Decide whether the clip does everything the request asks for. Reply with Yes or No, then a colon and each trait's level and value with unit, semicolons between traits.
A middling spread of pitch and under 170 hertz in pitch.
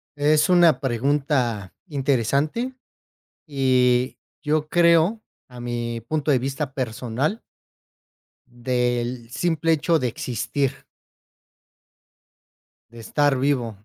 Yes: average, 3.8 semitones; low, 135 Hz